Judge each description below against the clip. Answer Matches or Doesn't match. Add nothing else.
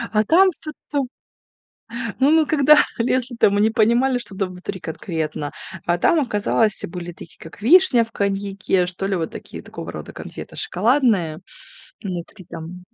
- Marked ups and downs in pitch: Matches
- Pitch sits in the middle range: Doesn't match